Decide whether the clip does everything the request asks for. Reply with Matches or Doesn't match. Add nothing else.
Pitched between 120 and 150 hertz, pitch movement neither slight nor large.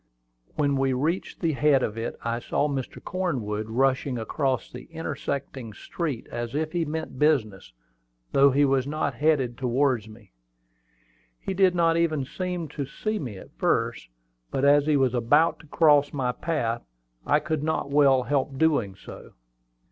Matches